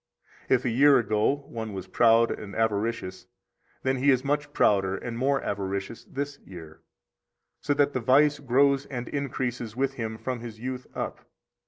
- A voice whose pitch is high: No, low, 125 Hz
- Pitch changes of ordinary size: Yes, average, 4.0 semitones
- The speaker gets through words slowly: No, average, 170 wpm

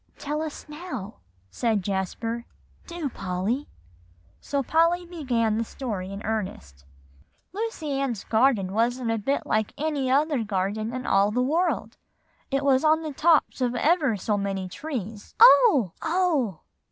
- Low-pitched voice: No, very high, 250 Hz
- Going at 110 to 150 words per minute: Yes, average, 145 wpm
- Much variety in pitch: Yes, wide, 6.4 semitones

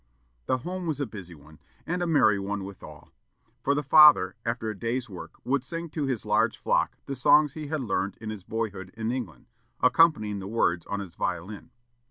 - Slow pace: No, average, 200 wpm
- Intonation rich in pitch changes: Yes, wide, 6.4 semitones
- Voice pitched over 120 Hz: No, low, 115 Hz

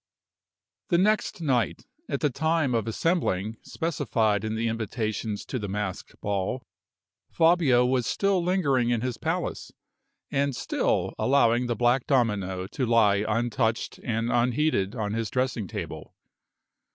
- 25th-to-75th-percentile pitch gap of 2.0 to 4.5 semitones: Yes, average, 4.2 semitones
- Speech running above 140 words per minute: No, slow, 135 wpm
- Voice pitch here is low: Yes, low, 120 Hz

